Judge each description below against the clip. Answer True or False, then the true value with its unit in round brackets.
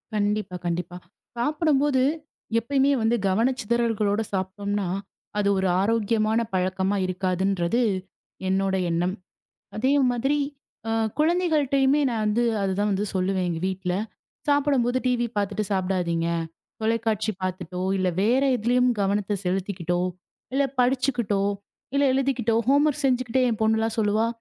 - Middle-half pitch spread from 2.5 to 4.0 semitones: False (4.8 semitones)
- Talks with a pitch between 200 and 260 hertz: True (215 Hz)